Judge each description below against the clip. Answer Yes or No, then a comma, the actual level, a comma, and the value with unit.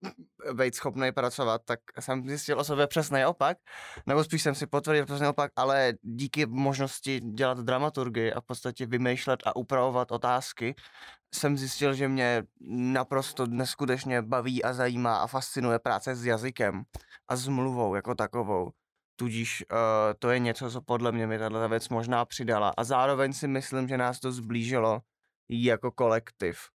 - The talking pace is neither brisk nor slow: Yes, average, 160 wpm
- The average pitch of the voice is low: Yes, low, 125 Hz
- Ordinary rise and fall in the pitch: No, narrow, 2.3 semitones